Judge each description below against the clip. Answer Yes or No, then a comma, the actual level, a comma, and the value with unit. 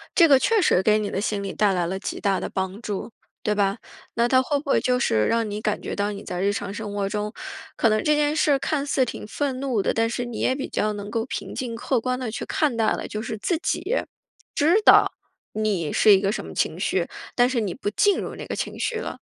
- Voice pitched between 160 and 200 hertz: No, high, 225 Hz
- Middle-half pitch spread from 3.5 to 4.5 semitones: Yes, average, 4.2 semitones